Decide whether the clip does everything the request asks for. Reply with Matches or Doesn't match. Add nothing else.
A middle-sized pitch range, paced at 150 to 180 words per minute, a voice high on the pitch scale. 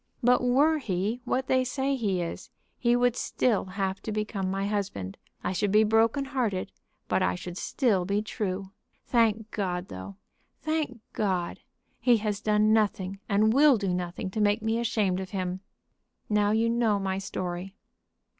Matches